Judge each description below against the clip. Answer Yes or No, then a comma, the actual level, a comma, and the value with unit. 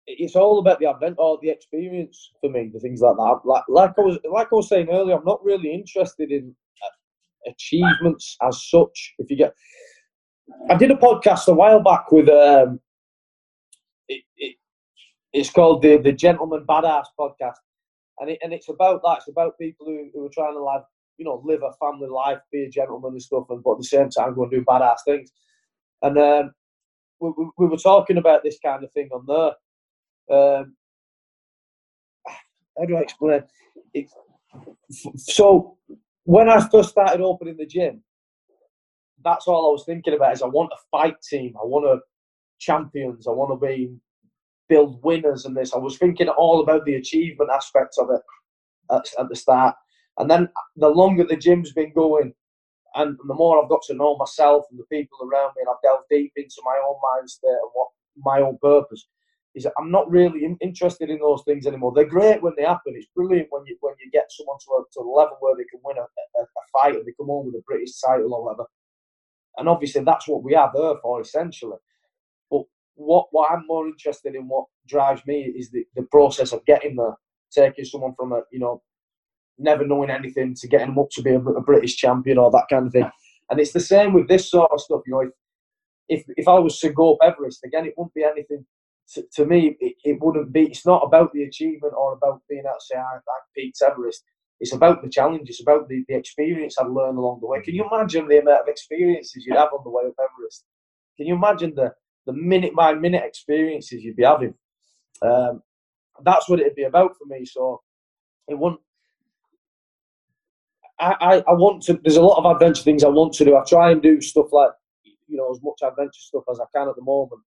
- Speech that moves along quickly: Yes, fast, 210 wpm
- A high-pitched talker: No, medium, 155 Hz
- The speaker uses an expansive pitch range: No, average, 4.7 semitones